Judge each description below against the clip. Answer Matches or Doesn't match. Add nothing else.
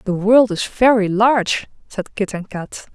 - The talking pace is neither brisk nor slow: Matches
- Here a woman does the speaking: Matches